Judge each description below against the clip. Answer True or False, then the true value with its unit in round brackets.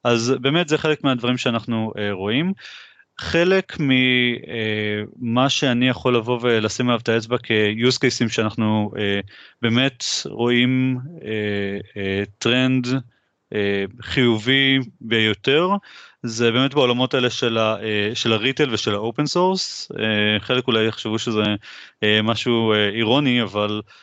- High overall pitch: False (120 Hz)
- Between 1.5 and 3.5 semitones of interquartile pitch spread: True (3.1 semitones)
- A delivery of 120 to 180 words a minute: True (125 wpm)